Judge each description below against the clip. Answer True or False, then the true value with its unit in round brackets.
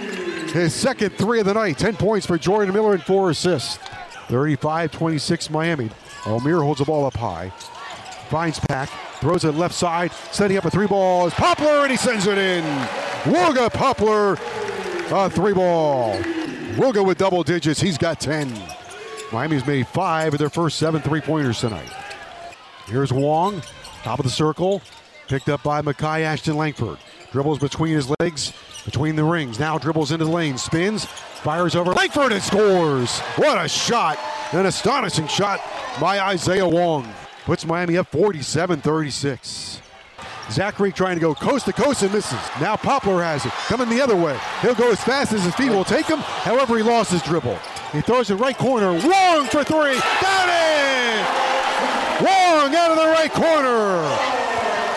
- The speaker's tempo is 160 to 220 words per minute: True (170 wpm)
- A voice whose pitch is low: False (175 Hz)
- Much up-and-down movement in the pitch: True (5.9 semitones)